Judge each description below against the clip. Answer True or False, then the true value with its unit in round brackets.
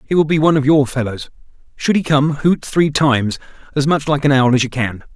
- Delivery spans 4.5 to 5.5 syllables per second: False (5.8 syllables/s)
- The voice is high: False (140 Hz)